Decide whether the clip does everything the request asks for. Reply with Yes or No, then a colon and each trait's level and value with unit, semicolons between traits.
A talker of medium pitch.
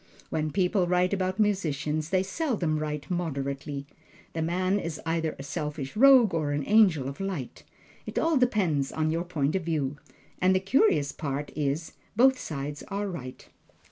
Yes: medium, 165 Hz